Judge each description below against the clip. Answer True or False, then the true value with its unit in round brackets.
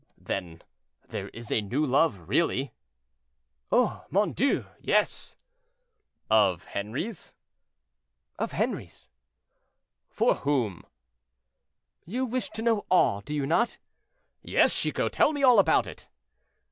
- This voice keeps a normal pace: False (115 wpm)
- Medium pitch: True (145 Hz)